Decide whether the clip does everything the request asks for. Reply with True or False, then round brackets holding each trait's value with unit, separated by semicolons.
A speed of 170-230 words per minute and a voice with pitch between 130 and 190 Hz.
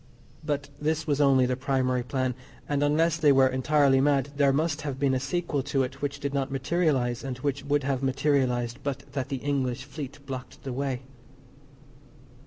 True (185 wpm; 140 Hz)